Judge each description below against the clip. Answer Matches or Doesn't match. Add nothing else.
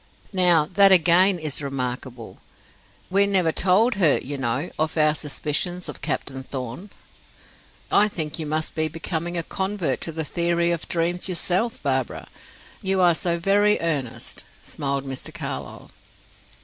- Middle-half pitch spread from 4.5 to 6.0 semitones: Doesn't match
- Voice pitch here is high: Doesn't match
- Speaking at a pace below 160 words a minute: Matches